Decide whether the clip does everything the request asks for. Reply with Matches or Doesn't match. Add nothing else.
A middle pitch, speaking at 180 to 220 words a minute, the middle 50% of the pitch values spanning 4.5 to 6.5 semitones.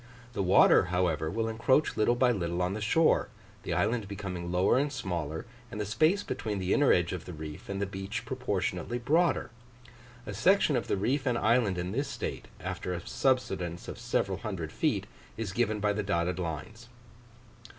Doesn't match